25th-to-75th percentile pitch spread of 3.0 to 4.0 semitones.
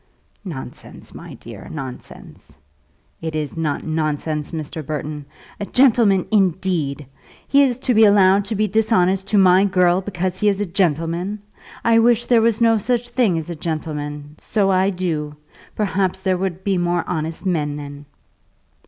No: average, 4.7 semitones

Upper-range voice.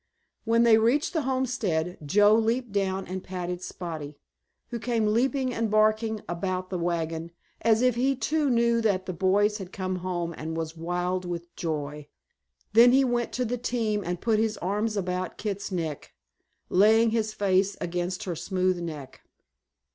Yes: high, 200 Hz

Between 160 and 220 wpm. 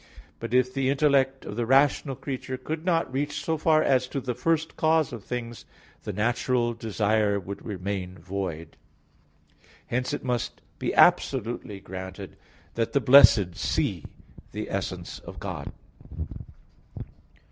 No: slow, 135 wpm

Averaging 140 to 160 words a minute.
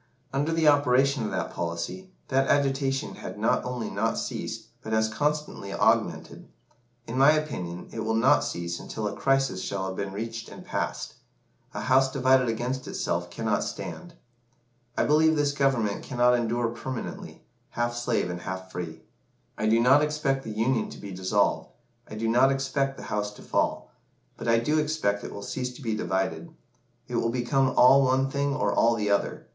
No: average, 180 wpm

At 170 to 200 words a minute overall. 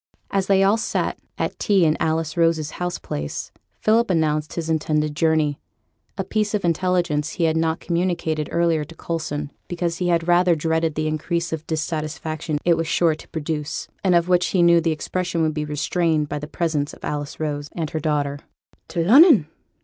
Yes: average, 190 wpm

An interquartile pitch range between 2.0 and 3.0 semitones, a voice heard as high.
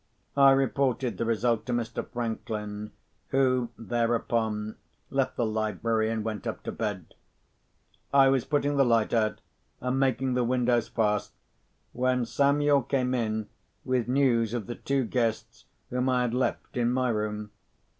No: average, 2.7 semitones; low, 120 Hz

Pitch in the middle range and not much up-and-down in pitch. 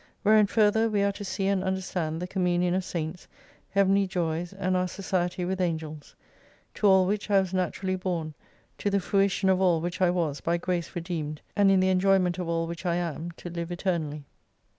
Yes: medium, 180 Hz; narrow, 2.2 semitones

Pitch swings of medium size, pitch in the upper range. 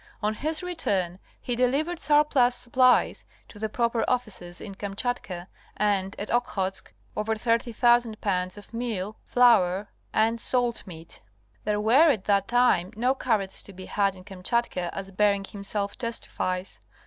Yes: average, 4.0 semitones; high, 215 Hz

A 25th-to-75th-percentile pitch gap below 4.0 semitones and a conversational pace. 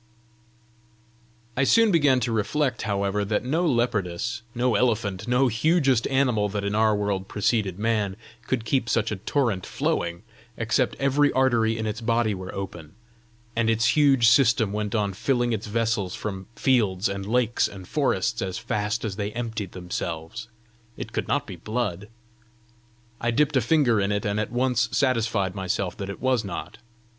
Yes: average, 3.5 semitones; average, 165 wpm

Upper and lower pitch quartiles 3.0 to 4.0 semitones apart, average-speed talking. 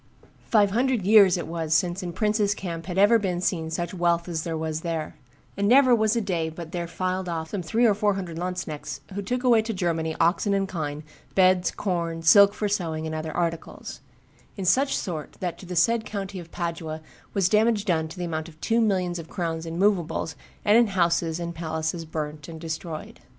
No: average, 3.6 semitones; fast, 210 wpm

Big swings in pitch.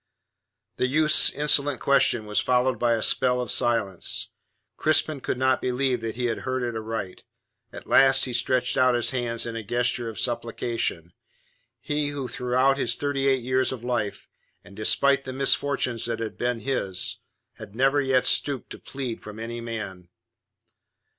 No: narrow, 2.5 semitones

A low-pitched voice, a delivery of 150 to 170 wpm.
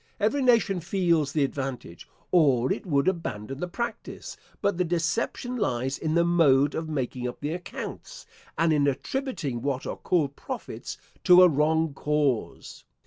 No: medium, 155 Hz; average, 155 wpm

